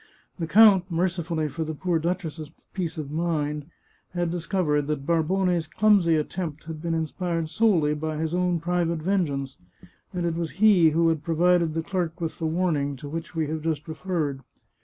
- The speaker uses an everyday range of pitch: No, narrow, 2.3 semitones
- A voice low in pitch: No, medium, 165 Hz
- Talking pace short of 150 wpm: No, average, 180 wpm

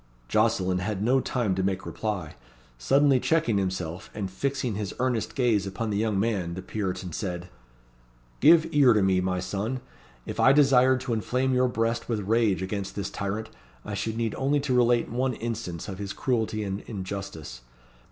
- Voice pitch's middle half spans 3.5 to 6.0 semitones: Yes, average, 4.6 semitones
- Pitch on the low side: Yes, low, 110 Hz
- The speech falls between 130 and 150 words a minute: No, average, 175 wpm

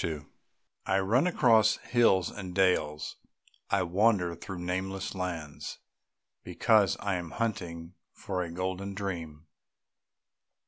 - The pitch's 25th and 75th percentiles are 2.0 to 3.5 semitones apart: Yes, average, 2.7 semitones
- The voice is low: Yes, very low, 95 Hz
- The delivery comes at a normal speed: No, slow, 110 wpm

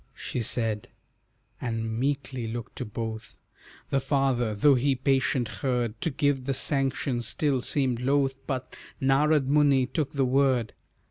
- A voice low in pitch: Yes, low, 130 Hz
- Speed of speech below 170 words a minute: Yes, average, 140 wpm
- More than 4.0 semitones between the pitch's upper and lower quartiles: No, narrow, 2.6 semitones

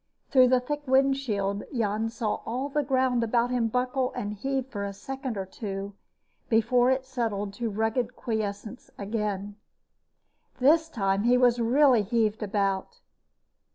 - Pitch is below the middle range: No, high, 235 Hz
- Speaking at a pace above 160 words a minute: No, average, 145 wpm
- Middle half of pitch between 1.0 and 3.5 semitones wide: No, average, 3.9 semitones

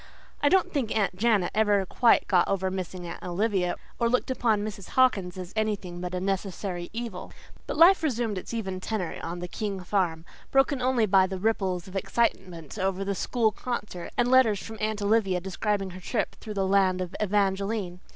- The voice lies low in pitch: No, high, 200 Hz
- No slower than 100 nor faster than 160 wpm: No, average, 190 wpm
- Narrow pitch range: No, average, 3.3 semitones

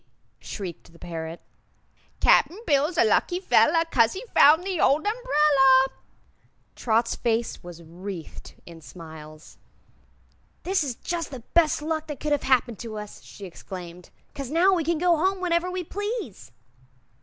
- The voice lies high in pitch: Yes, very high, 275 Hz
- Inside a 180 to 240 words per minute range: No, average, 150 wpm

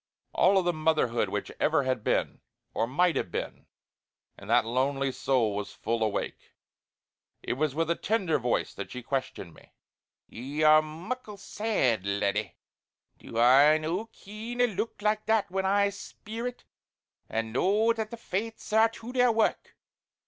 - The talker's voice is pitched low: No, medium, 160 Hz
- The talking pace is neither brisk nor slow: Yes, average, 160 wpm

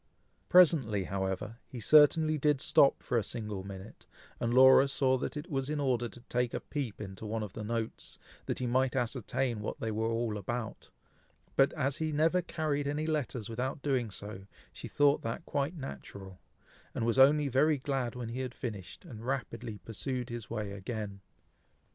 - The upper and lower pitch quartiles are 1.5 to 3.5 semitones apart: No, average, 4.3 semitones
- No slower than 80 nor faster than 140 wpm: No, average, 180 wpm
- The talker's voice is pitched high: No, low, 125 Hz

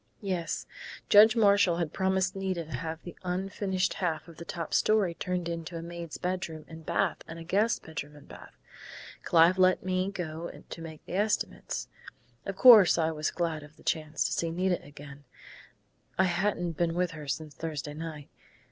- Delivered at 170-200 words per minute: Yes, average, 180 wpm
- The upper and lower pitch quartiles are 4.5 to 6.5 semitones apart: No, average, 2.7 semitones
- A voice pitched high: No, medium, 170 Hz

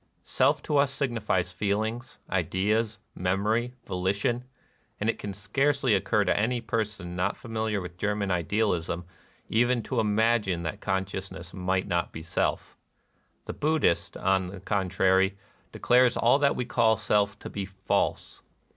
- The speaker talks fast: No, average, 145 wpm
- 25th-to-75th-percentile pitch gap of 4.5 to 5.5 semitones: No, average, 3.5 semitones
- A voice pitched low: Yes, low, 105 Hz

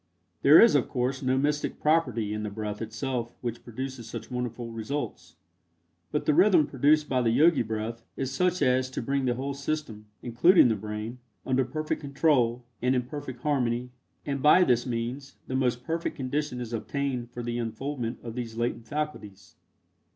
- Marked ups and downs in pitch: No, average, 3.5 semitones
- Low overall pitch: Yes, low, 125 Hz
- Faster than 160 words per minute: Yes, average, 175 wpm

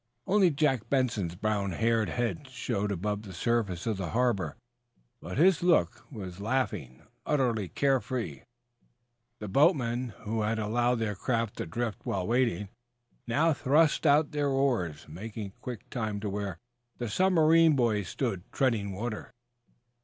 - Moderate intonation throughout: Yes, average, 4.6 semitones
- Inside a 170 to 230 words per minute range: No, average, 145 wpm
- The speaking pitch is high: No, low, 115 Hz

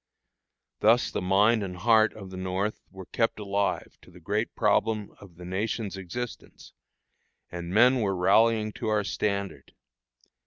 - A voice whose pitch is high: No, low, 100 Hz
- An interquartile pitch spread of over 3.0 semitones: No, average, 2.7 semitones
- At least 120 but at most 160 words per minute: Yes, average, 150 wpm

